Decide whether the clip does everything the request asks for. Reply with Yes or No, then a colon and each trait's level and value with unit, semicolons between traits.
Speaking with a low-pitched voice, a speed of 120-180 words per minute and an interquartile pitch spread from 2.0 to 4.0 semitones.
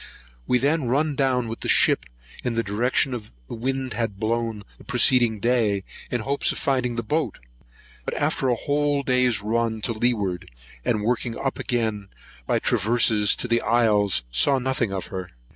Yes: low, 120 Hz; average, 170 wpm; average, 3.1 semitones